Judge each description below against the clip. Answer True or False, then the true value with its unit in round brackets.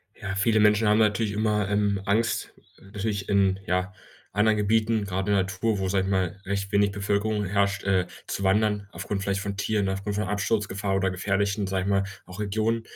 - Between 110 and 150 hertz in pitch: False (100 Hz)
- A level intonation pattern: True (1.5 semitones)